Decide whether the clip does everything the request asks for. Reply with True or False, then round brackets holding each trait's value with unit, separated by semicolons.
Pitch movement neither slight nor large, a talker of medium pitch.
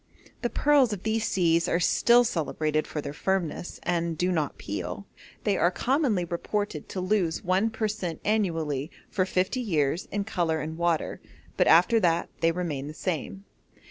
True (4.2 semitones; 180 Hz)